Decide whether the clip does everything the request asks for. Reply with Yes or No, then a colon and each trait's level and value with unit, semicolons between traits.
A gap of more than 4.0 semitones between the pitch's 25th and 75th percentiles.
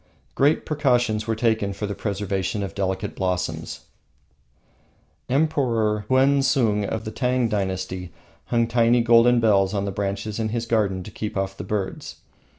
No: average, 3.3 semitones